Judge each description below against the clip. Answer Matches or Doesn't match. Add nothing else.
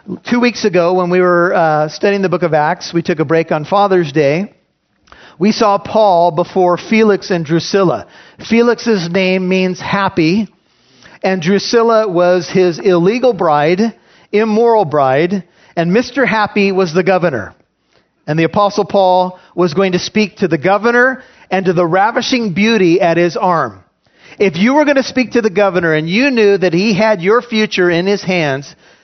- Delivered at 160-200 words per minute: Matches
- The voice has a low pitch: Doesn't match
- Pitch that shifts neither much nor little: Matches